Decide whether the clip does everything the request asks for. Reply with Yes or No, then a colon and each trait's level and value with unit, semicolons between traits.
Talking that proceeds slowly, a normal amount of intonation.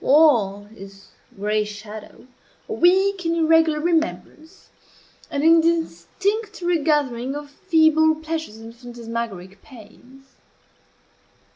No: slow, 95 wpm; wide, 6.6 semitones